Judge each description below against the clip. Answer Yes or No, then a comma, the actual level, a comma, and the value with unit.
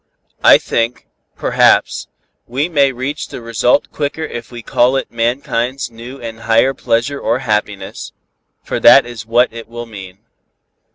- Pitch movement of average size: No, narrow, 2.3 semitones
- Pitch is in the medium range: No, low, 120 Hz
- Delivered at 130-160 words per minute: Yes, average, 150 wpm